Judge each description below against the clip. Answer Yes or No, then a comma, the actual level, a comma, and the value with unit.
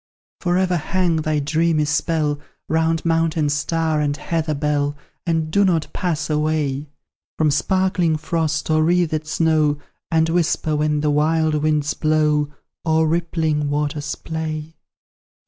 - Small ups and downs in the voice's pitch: Yes, narrow, 1.5 semitones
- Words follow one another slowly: Yes, slow, 130 wpm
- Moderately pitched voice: Yes, medium, 155 Hz